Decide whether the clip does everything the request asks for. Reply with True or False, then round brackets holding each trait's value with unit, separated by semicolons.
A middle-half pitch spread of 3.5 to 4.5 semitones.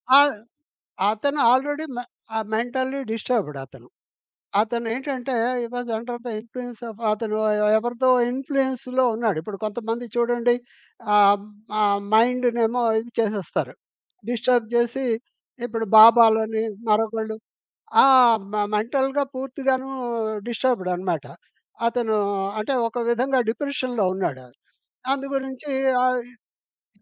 False (2.8 semitones)